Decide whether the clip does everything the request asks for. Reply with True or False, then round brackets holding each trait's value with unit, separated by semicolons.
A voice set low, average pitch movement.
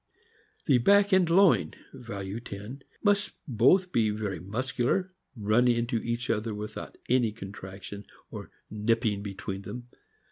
True (115 Hz; 4.1 semitones)